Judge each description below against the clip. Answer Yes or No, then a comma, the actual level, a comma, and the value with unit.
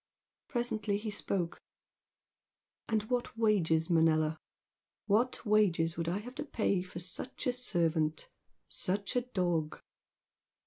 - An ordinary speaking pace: No, slow, 120 wpm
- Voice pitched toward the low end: No, high, 200 Hz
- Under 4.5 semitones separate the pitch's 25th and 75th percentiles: No, average, 5.1 semitones